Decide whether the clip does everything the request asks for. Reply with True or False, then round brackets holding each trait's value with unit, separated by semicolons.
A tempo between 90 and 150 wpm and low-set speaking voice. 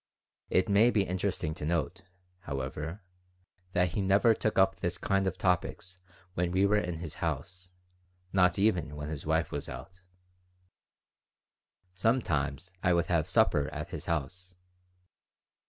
True (140 wpm; 90 Hz)